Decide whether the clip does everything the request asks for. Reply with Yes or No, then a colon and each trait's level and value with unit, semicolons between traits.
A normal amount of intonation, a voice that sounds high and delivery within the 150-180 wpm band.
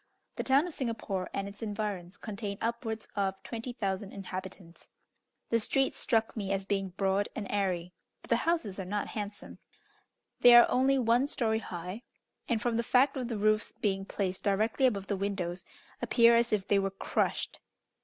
Yes: average, 3.2 semitones; high, 205 Hz; average, 175 wpm